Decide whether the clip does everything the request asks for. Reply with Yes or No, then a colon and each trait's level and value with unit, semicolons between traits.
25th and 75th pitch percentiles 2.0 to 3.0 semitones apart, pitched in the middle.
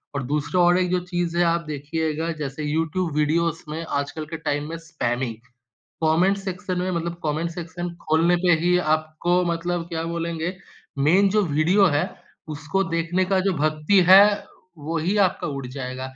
Yes: narrow, 2.6 semitones; medium, 165 Hz